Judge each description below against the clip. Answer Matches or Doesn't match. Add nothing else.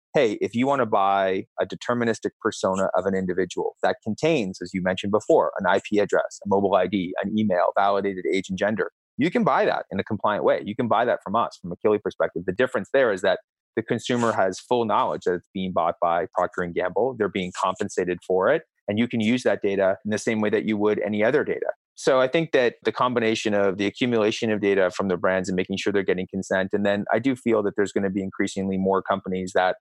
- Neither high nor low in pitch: Doesn't match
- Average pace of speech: Doesn't match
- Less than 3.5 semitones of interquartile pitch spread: Matches